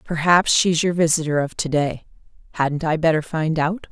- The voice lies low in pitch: No, medium, 160 Hz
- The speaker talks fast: No, average, 185 wpm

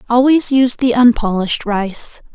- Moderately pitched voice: No, high, 235 Hz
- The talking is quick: No, slow, 130 wpm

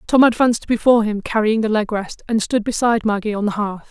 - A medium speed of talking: No, fast, 230 wpm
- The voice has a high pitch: Yes, high, 220 Hz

